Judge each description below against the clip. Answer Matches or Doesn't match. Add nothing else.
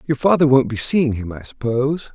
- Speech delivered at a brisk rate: Matches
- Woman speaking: Doesn't match